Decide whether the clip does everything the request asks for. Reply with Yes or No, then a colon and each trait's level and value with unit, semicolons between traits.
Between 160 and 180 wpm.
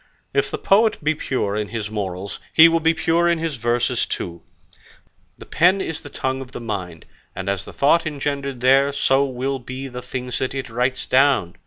No: average, 200 wpm